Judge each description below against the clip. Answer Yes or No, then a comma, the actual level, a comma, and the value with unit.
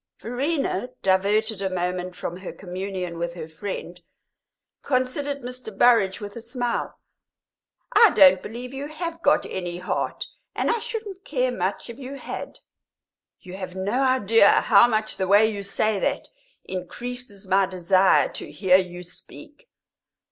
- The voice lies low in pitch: No, high, 205 Hz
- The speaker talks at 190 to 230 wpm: No, average, 150 wpm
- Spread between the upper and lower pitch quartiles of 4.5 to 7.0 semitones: Yes, average, 5.2 semitones